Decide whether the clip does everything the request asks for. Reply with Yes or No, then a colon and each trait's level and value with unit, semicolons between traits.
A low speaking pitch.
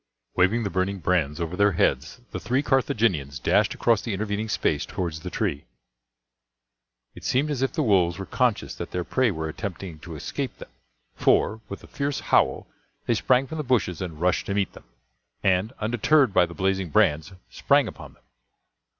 Yes: very low, 95 Hz